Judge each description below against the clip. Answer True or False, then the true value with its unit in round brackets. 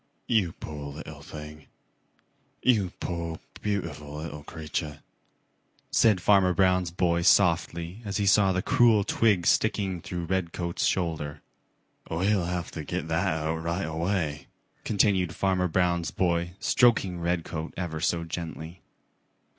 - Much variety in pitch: False (2.8 semitones)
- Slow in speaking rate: True (125 wpm)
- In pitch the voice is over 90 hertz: False (85 Hz)